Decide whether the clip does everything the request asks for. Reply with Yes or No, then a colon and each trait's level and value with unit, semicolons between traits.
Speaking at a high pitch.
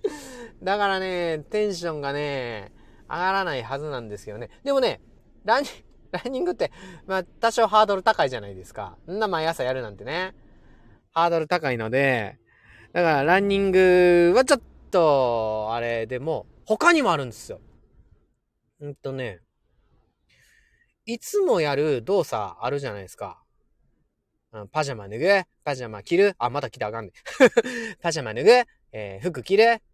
No: medium, 175 Hz